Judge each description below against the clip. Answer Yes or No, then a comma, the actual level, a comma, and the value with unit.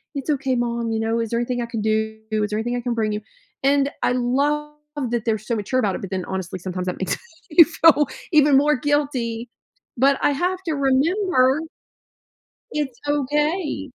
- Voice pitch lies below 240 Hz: No, very high, 250 Hz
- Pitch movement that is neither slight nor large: Yes, average, 4.7 semitones